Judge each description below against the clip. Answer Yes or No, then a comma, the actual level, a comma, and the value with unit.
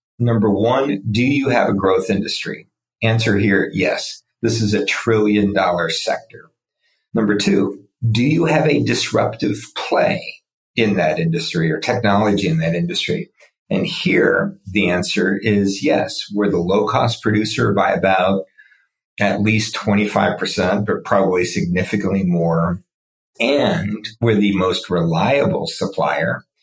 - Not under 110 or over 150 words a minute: Yes, slow, 135 wpm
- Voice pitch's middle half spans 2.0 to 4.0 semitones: Yes, average, 3.0 semitones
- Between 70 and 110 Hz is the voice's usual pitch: Yes, low, 105 Hz